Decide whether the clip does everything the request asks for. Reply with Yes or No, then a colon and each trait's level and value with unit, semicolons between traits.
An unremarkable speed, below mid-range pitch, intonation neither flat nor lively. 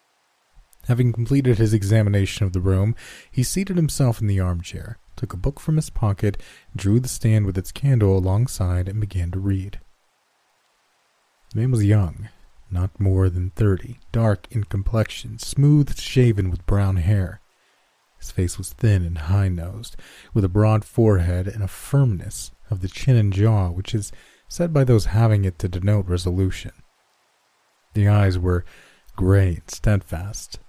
Yes: average, 160 wpm; low, 105 Hz; average, 3.4 semitones